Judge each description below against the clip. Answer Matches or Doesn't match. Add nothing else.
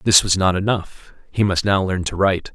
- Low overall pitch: Matches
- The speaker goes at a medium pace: Doesn't match